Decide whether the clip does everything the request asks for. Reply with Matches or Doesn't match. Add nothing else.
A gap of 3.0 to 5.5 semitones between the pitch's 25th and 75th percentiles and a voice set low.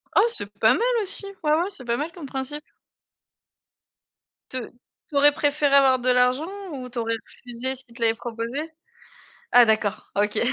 Doesn't match